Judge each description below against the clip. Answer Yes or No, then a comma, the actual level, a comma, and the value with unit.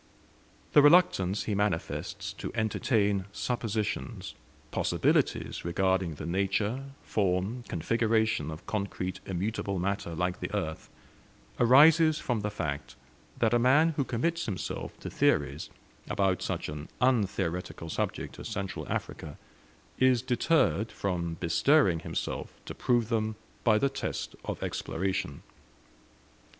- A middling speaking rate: No, slow, 120 wpm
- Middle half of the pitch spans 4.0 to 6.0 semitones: Yes, average, 4.9 semitones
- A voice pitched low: Yes, low, 100 Hz